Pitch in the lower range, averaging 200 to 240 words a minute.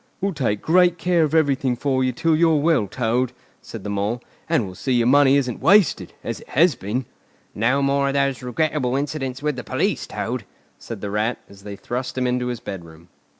Yes: low, 130 Hz; fast, 205 wpm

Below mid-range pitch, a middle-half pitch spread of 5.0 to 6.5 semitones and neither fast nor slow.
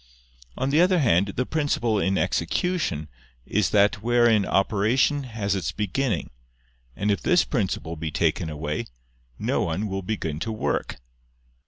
Yes: low, 105 Hz; wide, 5.5 semitones; average, 145 wpm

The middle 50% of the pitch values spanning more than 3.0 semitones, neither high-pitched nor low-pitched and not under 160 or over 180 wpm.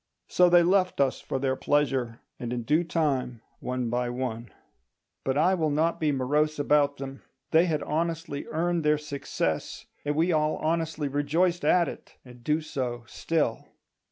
Yes: average, 3.9 semitones; medium, 150 Hz; average, 165 wpm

